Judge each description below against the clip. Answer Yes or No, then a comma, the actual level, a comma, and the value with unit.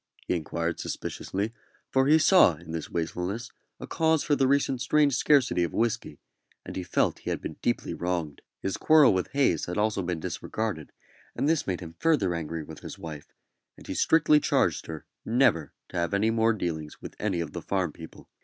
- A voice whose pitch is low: Yes, very low, 95 Hz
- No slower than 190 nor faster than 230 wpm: Yes, average, 195 wpm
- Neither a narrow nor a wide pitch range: No, wide, 8.0 semitones